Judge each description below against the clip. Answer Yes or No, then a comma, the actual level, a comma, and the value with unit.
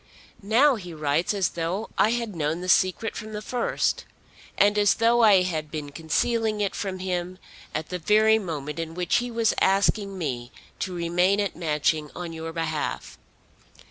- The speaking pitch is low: No, medium, 185 Hz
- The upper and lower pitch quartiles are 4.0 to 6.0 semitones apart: Yes, average, 4.5 semitones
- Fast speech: No, average, 175 wpm